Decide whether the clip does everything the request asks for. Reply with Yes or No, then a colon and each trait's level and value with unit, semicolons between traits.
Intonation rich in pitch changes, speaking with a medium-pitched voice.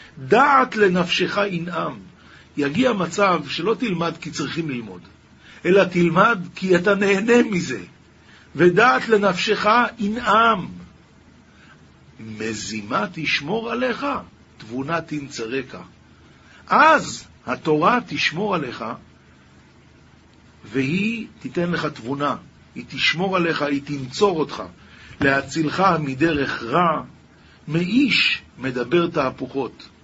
Yes: wide, 6.8 semitones; medium, 165 Hz